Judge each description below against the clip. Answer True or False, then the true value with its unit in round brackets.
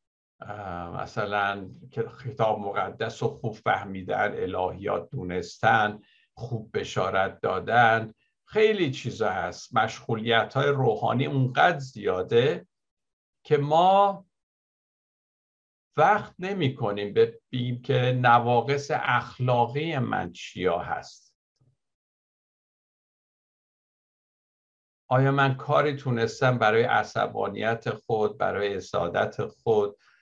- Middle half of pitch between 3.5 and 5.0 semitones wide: True (4.7 semitones)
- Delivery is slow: True (80 wpm)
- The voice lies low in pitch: True (125 Hz)